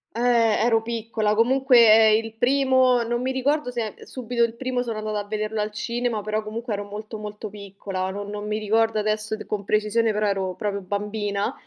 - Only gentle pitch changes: Yes, narrow, 2.1 semitones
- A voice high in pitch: Yes, high, 215 Hz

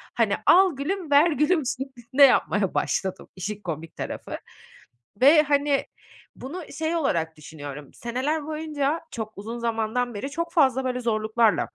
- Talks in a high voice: Yes, very high, 255 Hz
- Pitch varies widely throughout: Yes, wide, 5.7 semitones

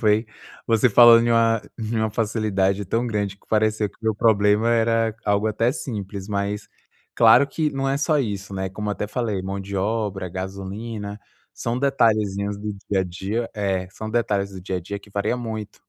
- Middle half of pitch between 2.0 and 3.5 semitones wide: Yes, narrow, 2.5 semitones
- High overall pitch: No, low, 105 Hz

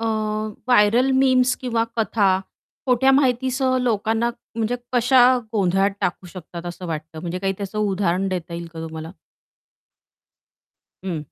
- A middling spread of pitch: No, wide, 5.8 semitones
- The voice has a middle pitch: No, high, 205 Hz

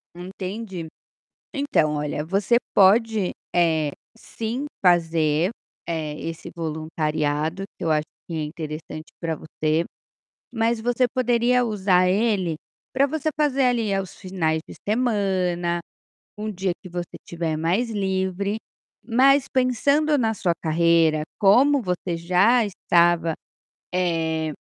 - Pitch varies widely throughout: Yes, wide, 5.7 semitones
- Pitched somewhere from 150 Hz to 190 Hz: Yes, medium, 185 Hz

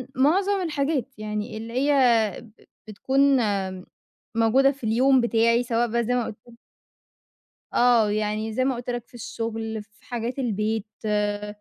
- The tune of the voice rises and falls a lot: No, average, 2.9 semitones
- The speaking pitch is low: No, high, 230 Hz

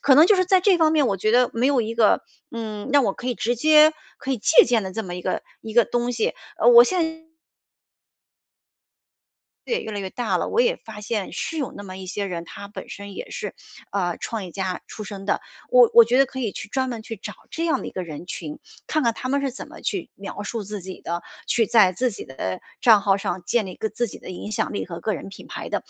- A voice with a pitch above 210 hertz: Yes, high, 225 Hz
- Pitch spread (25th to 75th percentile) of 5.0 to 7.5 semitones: Yes, wide, 5.4 semitones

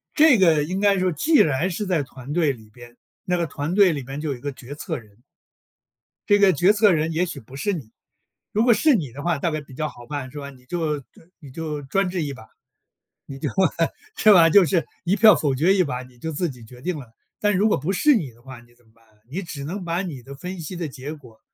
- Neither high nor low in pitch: Yes, medium, 155 Hz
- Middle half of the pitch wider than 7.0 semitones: No, wide, 5.5 semitones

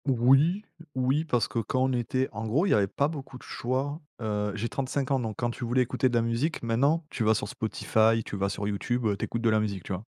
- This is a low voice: Yes, low, 120 Hz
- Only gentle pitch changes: No, average, 3.3 semitones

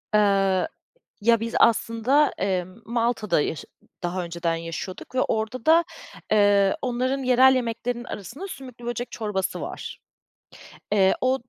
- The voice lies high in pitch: Yes, high, 225 Hz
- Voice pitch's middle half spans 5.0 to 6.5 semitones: No, average, 4.5 semitones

